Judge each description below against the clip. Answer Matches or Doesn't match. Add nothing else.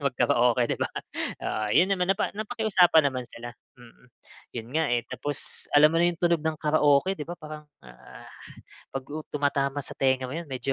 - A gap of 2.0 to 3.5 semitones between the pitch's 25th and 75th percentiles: Doesn't match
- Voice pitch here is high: Doesn't match